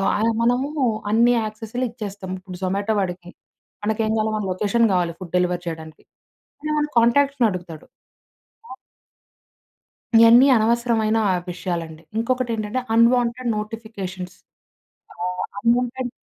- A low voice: No, high, 220 Hz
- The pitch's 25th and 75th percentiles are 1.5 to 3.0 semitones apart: No, average, 4.4 semitones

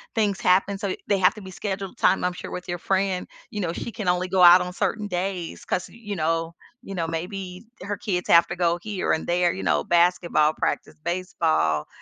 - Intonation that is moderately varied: No, narrow, 2.2 semitones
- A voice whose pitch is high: No, medium, 180 Hz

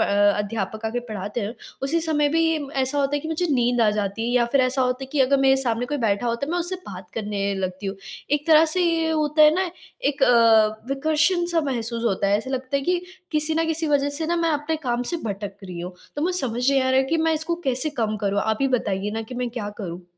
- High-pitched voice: Yes, very high, 260 Hz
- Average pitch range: No, wide, 6.1 semitones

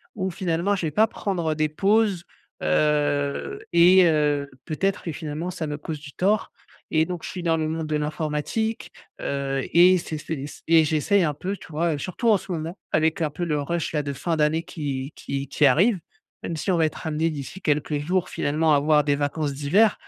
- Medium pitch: Yes, medium, 160 Hz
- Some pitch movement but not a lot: Yes, average, 3.1 semitones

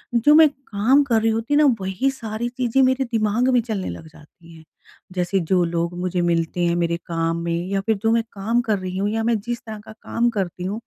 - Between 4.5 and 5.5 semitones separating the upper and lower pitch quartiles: Yes, average, 5.1 semitones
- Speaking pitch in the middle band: No, high, 210 Hz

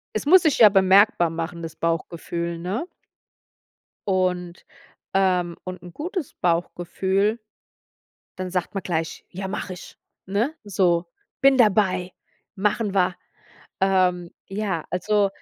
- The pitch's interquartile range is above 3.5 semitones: No, average, 2.7 semitones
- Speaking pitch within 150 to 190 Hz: Yes, medium, 185 Hz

